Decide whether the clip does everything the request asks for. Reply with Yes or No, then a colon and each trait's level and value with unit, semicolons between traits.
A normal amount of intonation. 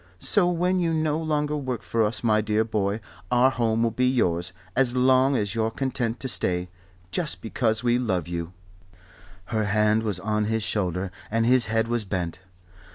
Yes: average, 3.4 semitones